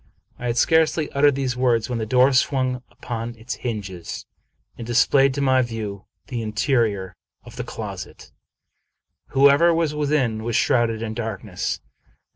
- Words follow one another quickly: No, average, 145 wpm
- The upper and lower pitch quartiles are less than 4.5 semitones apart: Yes, average, 3.5 semitones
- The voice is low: Yes, low, 120 Hz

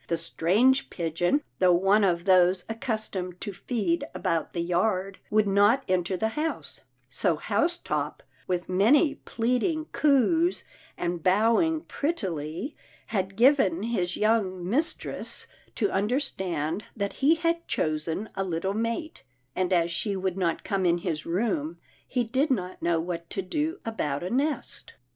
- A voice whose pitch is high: Yes, high, 195 Hz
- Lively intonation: Yes, wide, 5.9 semitones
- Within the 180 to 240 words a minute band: No, average, 145 wpm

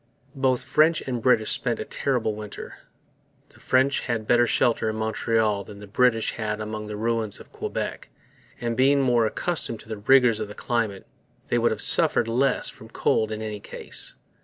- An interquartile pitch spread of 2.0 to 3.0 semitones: Yes, narrow, 2.6 semitones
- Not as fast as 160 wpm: No, average, 185 wpm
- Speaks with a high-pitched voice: No, low, 115 Hz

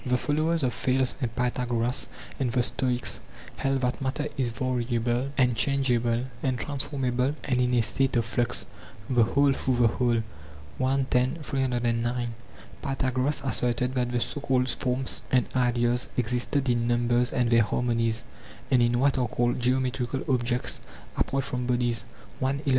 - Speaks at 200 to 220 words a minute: No, average, 155 wpm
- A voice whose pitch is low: Yes, low, 125 Hz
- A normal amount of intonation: No, narrow, 1.7 semitones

